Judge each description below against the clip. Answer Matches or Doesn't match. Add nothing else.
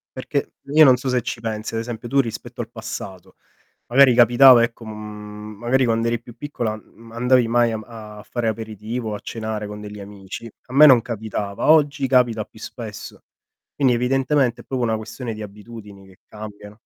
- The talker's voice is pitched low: Matches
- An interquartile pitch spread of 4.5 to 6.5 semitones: Doesn't match